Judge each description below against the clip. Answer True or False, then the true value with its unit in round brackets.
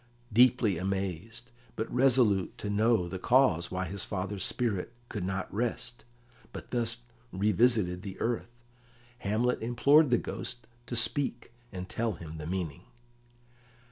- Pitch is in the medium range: False (110 Hz)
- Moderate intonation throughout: True (4.3 semitones)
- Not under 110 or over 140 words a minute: True (135 wpm)